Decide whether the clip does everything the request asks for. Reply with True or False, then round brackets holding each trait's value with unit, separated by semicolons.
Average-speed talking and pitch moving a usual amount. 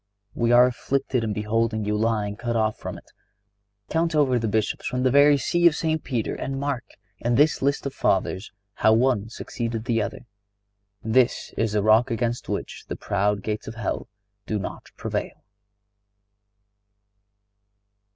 True (160 wpm; 3.4 semitones)